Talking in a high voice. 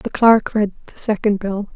Yes: high, 210 Hz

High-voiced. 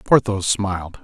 No: very low, 95 Hz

